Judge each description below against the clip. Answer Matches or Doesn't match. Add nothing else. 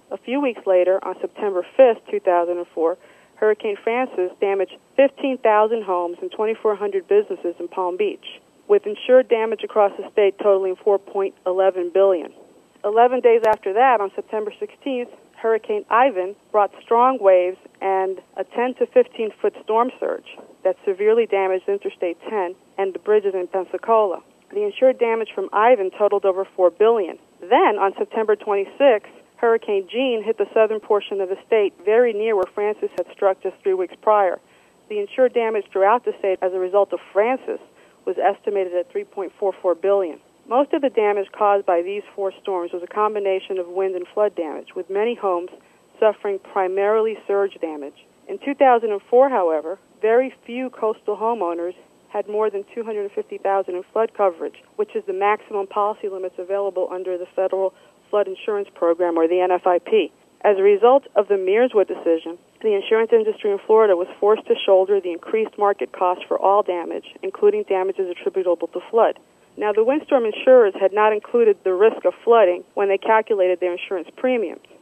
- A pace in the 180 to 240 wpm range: Doesn't match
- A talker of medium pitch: Doesn't match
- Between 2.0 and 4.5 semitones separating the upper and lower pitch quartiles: Doesn't match